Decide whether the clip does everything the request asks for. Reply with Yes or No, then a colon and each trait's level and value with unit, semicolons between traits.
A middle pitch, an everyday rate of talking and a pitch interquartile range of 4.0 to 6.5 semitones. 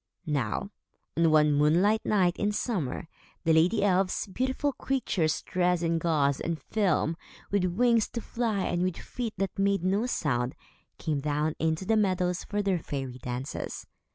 Yes: medium, 180 Hz; average, 155 wpm; average, 4.9 semitones